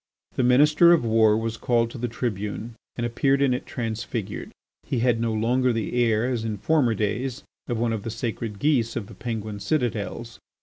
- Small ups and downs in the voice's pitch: Yes, narrow, 2.1 semitones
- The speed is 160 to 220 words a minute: Yes, average, 190 wpm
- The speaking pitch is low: Yes, low, 115 Hz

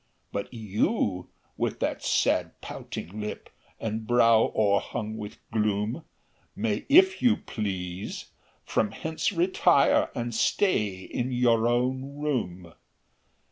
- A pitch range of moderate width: Yes, average, 4.2 semitones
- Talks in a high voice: No, low, 115 Hz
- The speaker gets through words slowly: Yes, slow, 110 wpm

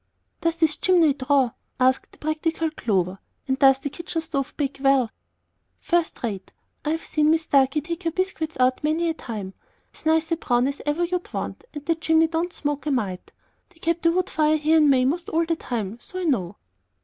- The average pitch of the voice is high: Yes, very high, 305 Hz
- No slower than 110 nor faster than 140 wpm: No, fast, 205 wpm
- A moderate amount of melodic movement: Yes, average, 3.8 semitones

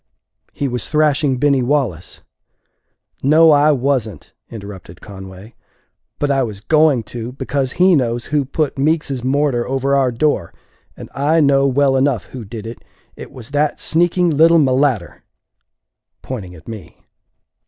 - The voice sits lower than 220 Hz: Yes, low, 135 Hz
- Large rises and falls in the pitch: No, average, 3.9 semitones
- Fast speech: No, average, 145 wpm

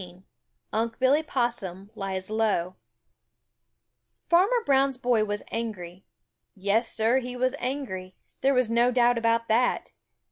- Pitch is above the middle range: Yes, high, 230 Hz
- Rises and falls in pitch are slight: No, average, 4.1 semitones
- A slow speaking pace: Yes, slow, 130 wpm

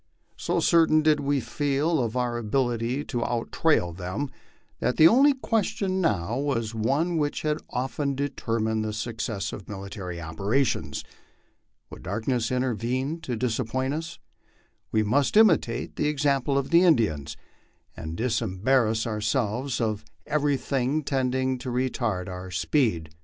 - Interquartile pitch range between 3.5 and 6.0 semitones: Yes, average, 4.7 semitones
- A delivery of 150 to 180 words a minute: No, average, 140 wpm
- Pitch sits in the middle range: No, low, 125 Hz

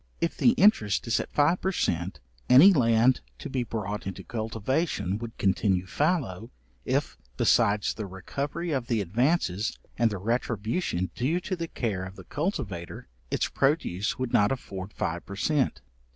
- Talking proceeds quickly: No, average, 160 wpm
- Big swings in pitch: Yes, wide, 6.8 semitones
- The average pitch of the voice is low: Yes, low, 115 Hz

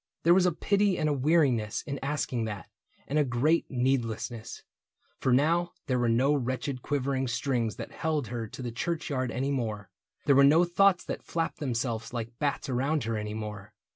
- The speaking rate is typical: Yes, average, 185 wpm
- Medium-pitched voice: No, low, 130 Hz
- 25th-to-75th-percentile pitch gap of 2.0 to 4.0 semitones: No, average, 4.4 semitones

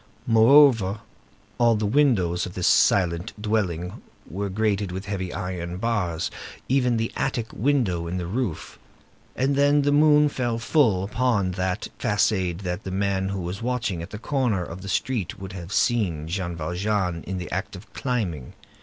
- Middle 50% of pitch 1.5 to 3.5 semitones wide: No, average, 4.6 semitones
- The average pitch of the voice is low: Yes, low, 100 Hz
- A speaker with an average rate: Yes, average, 165 wpm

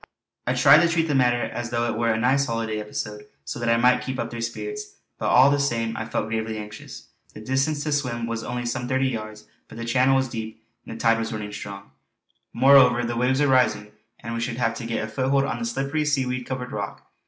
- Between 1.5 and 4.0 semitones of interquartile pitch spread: Yes, average, 2.7 semitones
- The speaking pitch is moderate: No, low, 120 Hz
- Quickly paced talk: Yes, fast, 235 wpm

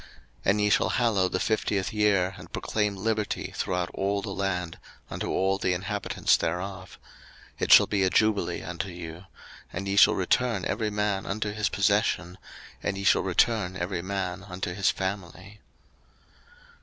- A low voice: Yes, very low, 95 Hz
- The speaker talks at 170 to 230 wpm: No, average, 160 wpm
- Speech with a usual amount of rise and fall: No, narrow, 2.2 semitones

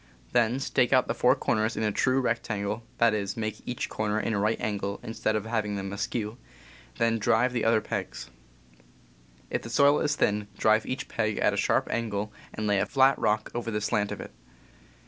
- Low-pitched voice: Yes, low, 110 Hz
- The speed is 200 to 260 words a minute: Yes, fast, 205 wpm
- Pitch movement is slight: Yes, narrow, 2.0 semitones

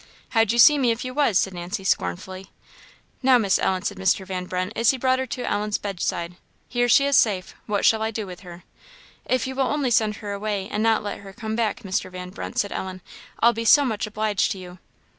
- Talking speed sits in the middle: No, fast, 235 wpm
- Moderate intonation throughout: Yes, average, 4.0 semitones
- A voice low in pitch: No, high, 210 Hz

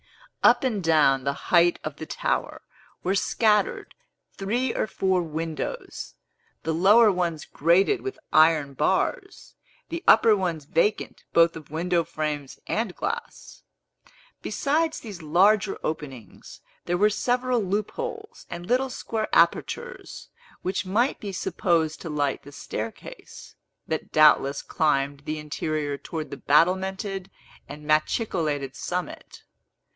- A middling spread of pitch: No, wide, 5.8 semitones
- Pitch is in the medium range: Yes, medium, 175 Hz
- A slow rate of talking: Yes, slow, 125 wpm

